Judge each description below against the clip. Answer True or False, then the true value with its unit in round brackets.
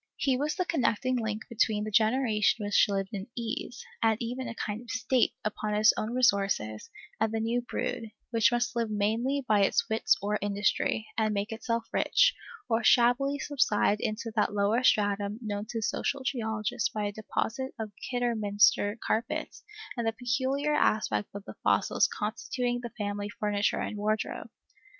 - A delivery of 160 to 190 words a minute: True (165 wpm)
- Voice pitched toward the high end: True (220 Hz)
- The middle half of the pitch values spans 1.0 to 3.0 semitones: True (2.7 semitones)